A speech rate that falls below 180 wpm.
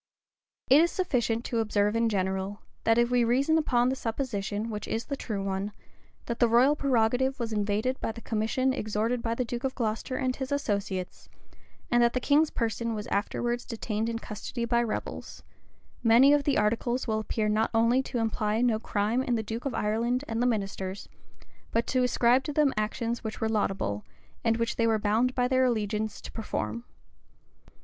No: average, 190 wpm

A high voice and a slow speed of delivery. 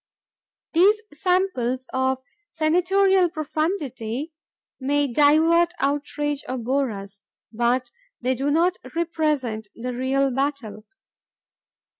Yes: very high, 285 Hz; slow, 95 wpm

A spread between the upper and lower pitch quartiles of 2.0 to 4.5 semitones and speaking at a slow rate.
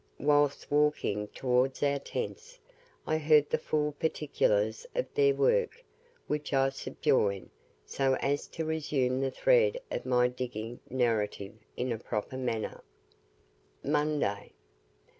Yes: average, 4.1 semitones; slow, 120 wpm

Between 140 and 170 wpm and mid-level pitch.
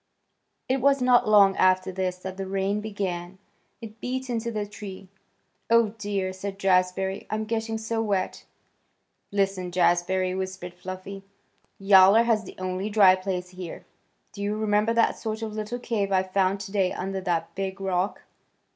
No: average, 155 wpm; high, 195 Hz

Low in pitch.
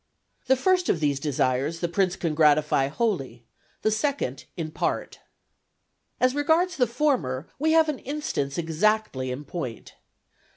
No: medium, 170 Hz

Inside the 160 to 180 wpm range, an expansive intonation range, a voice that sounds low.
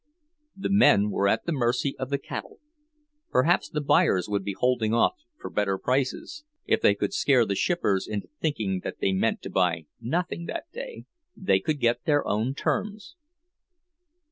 Yes: average, 170 wpm; wide, 8.3 semitones; low, 125 Hz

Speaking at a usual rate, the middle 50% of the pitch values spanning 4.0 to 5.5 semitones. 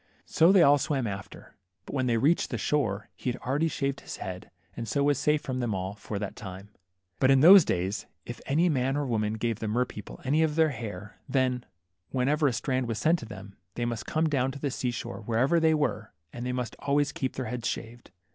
No: fast, 230 wpm; average, 4.6 semitones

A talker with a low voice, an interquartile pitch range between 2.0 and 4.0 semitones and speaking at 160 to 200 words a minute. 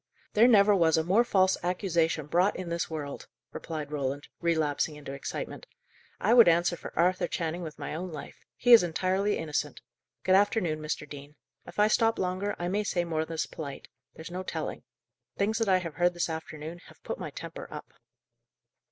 No: medium, 175 Hz; average, 3.5 semitones; average, 185 wpm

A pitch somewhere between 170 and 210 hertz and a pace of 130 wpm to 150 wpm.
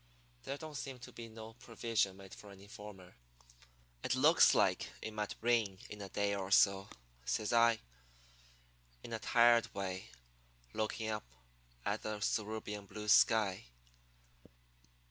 No: low, 105 Hz; average, 140 wpm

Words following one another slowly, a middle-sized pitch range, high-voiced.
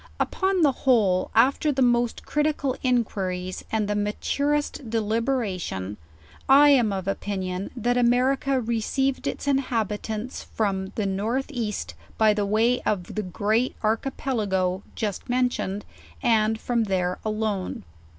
Yes: slow, 125 wpm; average, 4.1 semitones; high, 220 Hz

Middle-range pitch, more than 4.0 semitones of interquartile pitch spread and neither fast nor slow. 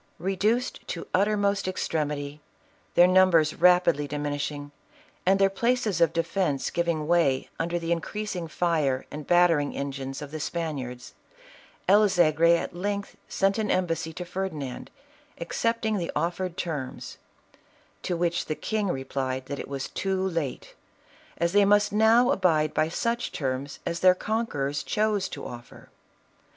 Yes: medium, 170 Hz; average, 4.8 semitones; average, 150 wpm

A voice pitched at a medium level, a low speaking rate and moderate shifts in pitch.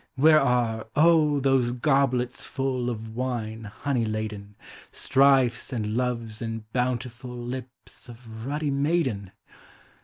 No: low, 125 Hz; slow, 115 wpm; average, 3.1 semitones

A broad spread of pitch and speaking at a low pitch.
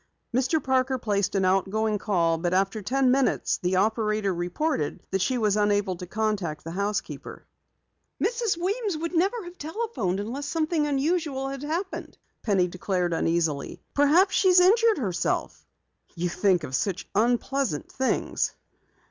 No: wide, 8.3 semitones; high, 220 Hz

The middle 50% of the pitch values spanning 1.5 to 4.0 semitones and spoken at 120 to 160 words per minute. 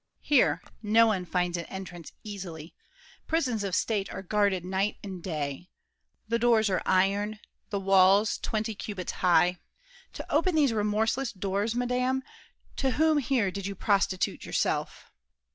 Yes: average, 3.6 semitones; average, 140 wpm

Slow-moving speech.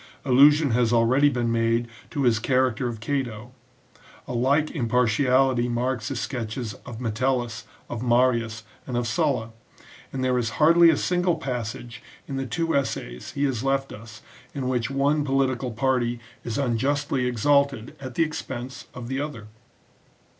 No: average, 155 wpm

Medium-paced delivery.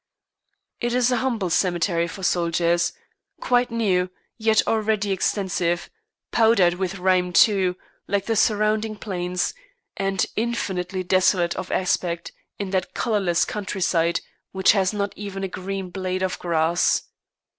No: slow, 130 wpm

